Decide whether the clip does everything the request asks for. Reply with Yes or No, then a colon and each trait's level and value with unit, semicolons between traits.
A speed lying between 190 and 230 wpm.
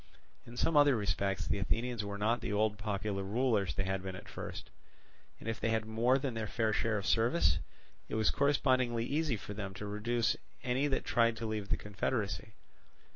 Yes: average, 195 wpm